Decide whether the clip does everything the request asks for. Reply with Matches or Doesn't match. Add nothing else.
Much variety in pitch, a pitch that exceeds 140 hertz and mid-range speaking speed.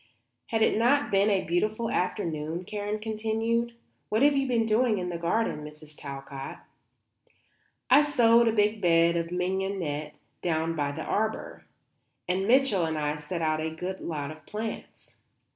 Matches